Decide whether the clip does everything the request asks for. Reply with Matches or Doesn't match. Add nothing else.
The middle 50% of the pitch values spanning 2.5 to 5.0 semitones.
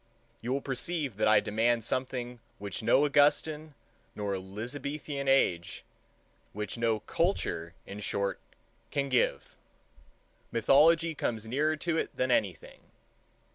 Doesn't match